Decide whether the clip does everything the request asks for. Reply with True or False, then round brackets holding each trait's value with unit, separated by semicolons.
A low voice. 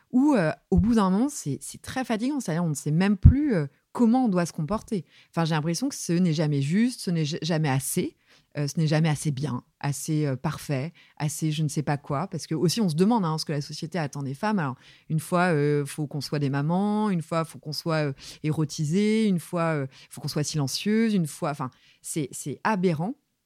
False (160 Hz)